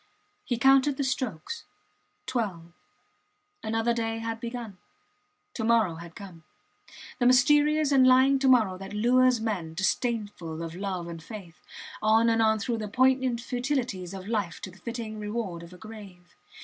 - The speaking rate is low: No, average, 155 wpm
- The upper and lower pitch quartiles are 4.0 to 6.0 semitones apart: Yes, average, 4.9 semitones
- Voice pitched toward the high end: Yes, high, 225 Hz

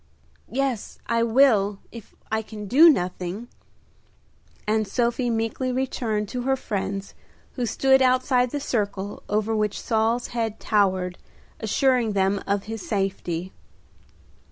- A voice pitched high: Yes, high, 220 Hz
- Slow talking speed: Yes, slow, 125 wpm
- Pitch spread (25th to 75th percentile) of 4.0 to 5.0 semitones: No, average, 3.6 semitones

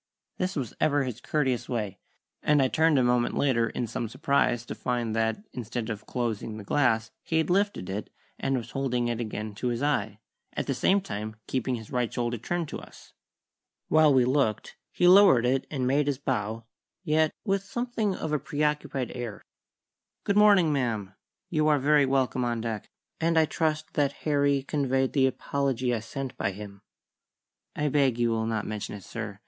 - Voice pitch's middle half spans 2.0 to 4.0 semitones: No, average, 4.6 semitones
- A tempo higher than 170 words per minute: Yes, average, 185 wpm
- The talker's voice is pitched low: Yes, low, 130 Hz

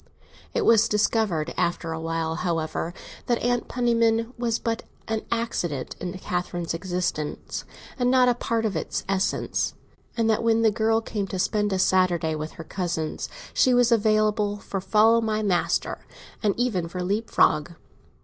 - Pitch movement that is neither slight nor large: Yes, average, 4.6 semitones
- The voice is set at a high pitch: Yes, high, 210 Hz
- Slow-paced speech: No, average, 160 wpm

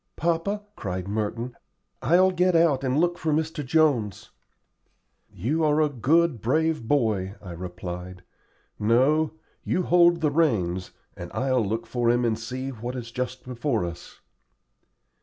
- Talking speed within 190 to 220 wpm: No, average, 140 wpm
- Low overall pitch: Yes, low, 130 Hz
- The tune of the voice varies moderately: No, wide, 6.4 semitones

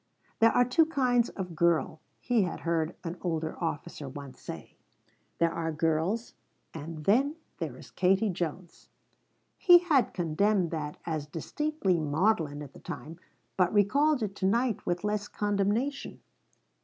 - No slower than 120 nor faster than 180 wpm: Yes, average, 145 wpm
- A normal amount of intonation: No, wide, 5.9 semitones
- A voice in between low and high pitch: Yes, medium, 180 Hz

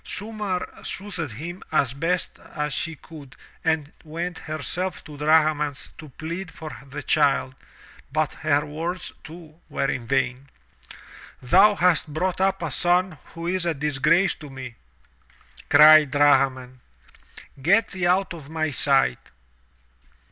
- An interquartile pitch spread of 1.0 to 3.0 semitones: No, average, 3.7 semitones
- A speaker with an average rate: No, slow, 130 wpm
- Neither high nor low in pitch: Yes, medium, 155 Hz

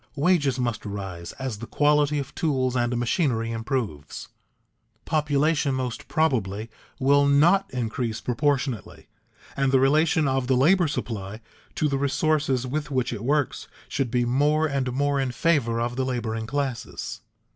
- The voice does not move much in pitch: No, average, 3.6 semitones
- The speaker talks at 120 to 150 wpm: Yes, average, 145 wpm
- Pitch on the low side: Yes, low, 130 Hz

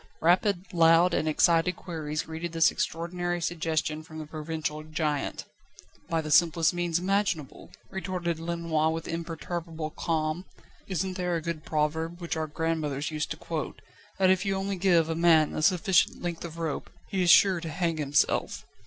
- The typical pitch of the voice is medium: Yes, medium, 165 Hz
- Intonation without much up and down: Yes, narrow, 1.9 semitones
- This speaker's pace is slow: No, average, 165 wpm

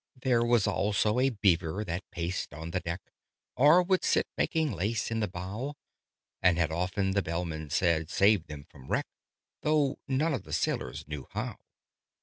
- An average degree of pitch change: No, wide, 6.2 semitones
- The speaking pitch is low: Yes, very low, 95 Hz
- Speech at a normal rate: Yes, average, 170 wpm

